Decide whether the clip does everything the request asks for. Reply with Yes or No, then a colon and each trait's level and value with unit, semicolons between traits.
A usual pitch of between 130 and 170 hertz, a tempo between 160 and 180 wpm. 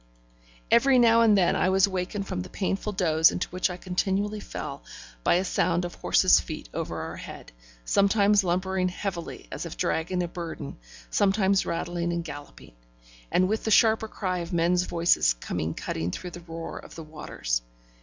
No: medium, 180 Hz; average, 175 wpm